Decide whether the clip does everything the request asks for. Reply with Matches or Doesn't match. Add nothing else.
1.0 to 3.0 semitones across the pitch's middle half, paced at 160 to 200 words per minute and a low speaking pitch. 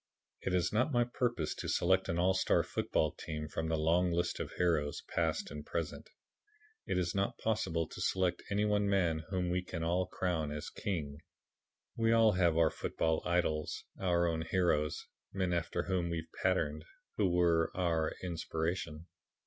Matches